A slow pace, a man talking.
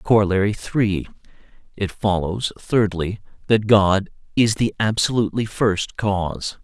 Yes: slow, 100 wpm; male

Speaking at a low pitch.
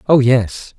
Yes: low, 125 Hz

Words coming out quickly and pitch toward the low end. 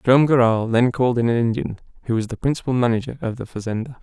Yes: fast, 225 wpm; low, 120 Hz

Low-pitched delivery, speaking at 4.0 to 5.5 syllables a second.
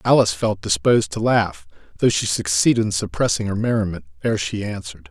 No: low, 100 Hz; 6.0 syllables/s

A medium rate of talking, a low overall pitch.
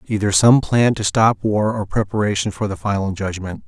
Yes: average, 195 wpm; low, 105 Hz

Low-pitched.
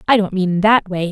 No: high, 195 Hz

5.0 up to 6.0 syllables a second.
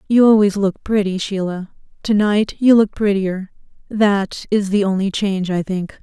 No: 4.6 syllables/s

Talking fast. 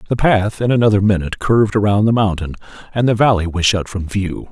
Yes: fast, 215 wpm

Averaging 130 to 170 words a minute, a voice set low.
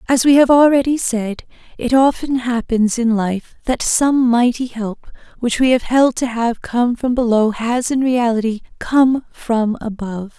No: average, 165 wpm; high, 240 Hz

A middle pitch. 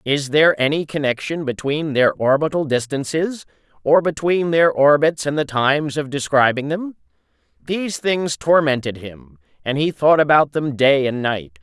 Yes: medium, 145 Hz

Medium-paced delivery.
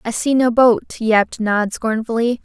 Yes: average, 170 wpm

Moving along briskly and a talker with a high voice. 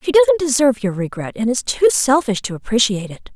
Yes: fast, 215 wpm; high, 245 Hz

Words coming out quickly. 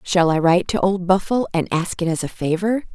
Yes: fast, 245 wpm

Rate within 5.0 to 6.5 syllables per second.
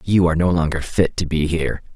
Yes: 6.3 syllables/s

